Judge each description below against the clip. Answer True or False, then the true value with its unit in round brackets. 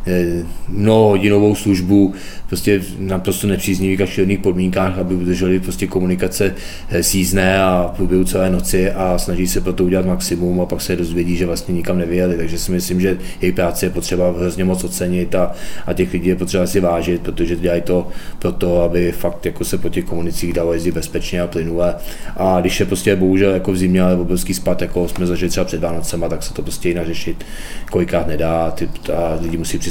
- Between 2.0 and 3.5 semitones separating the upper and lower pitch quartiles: False (1.3 semitones)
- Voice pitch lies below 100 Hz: True (90 Hz)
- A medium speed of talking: False (195 wpm)